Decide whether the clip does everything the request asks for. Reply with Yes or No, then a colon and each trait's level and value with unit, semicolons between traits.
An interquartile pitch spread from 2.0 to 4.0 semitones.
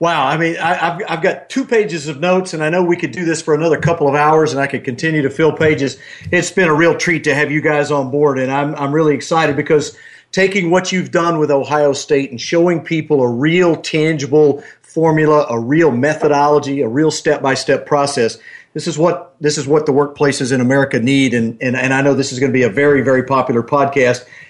Yes: average, 2.9 semitones